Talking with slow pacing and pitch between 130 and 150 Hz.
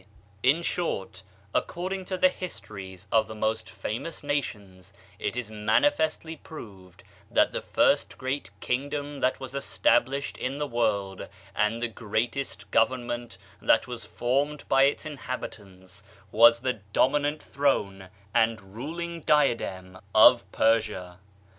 No: slow, 125 wpm; low, 120 Hz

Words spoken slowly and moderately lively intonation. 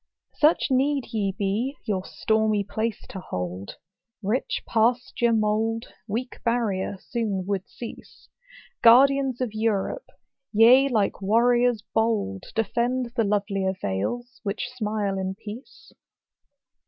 Yes: slow, 115 wpm; average, 3.4 semitones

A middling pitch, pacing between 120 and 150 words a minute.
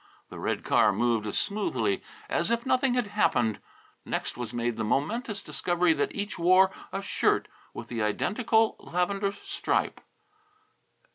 Yes: medium, 180 Hz; average, 145 wpm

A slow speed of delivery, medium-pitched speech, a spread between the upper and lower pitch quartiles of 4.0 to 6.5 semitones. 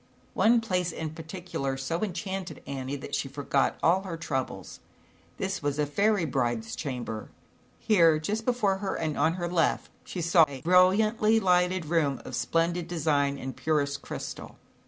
No: average, 155 wpm; medium, 165 Hz; average, 4.7 semitones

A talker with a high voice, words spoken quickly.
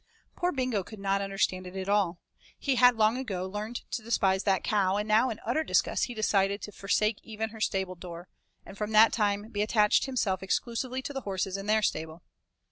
Yes: high, 210 Hz; fast, 210 wpm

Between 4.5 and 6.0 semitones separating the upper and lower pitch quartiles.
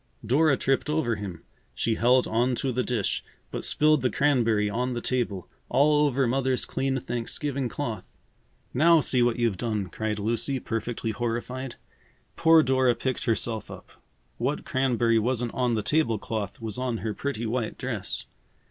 No: average, 2.9 semitones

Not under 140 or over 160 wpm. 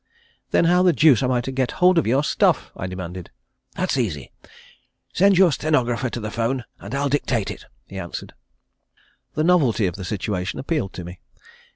No: average, 185 wpm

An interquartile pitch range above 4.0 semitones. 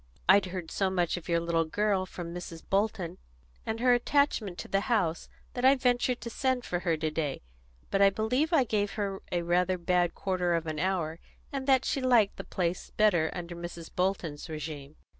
Yes: average, 4.5 semitones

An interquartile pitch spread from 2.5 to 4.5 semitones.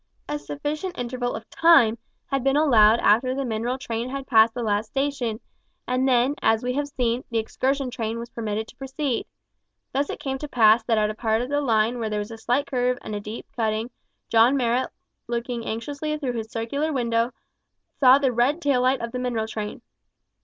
Yes: average, 3.3 semitones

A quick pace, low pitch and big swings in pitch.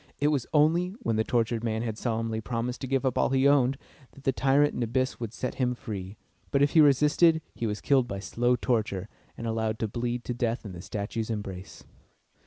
No: fast, 210 wpm; low, 120 Hz; average, 3.5 semitones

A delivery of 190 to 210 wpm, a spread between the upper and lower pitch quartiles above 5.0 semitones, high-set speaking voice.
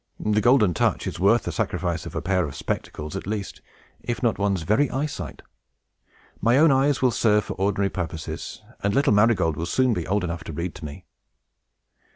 No: average, 195 wpm; wide, 5.6 semitones; low, 100 Hz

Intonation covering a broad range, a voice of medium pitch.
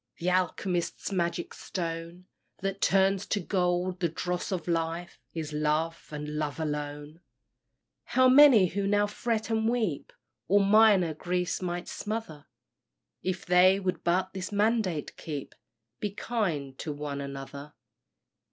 No: average, 4.0 semitones; medium, 180 Hz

